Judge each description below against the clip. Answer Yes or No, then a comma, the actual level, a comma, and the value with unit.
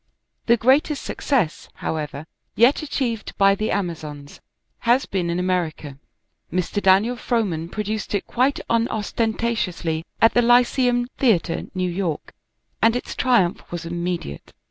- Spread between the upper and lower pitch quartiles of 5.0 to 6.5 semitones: Yes, wide, 5.6 semitones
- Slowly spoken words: Yes, slow, 125 wpm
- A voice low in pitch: No, high, 205 Hz